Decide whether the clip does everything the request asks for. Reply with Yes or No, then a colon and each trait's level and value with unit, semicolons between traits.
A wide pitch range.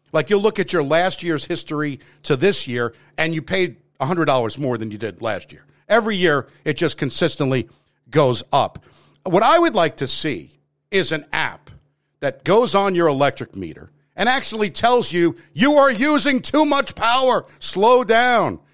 Yes: wide, 8.0 semitones